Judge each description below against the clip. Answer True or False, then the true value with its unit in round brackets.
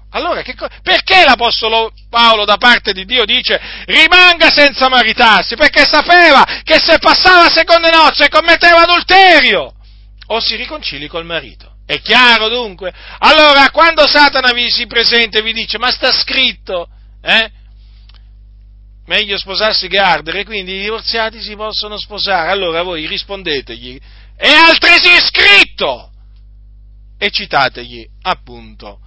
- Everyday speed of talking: True (135 wpm)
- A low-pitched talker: False (225 Hz)